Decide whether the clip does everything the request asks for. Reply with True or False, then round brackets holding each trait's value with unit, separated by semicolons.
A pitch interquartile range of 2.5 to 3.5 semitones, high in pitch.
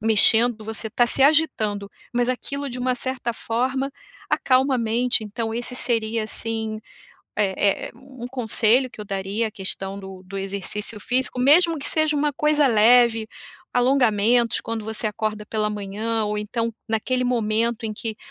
True (2.9 semitones; 230 Hz)